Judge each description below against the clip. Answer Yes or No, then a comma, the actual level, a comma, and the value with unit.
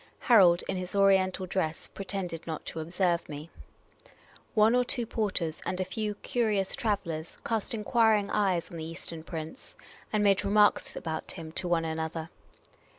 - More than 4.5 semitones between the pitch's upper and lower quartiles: No, average, 4.1 semitones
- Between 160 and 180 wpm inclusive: Yes, average, 165 wpm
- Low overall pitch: No, medium, 185 Hz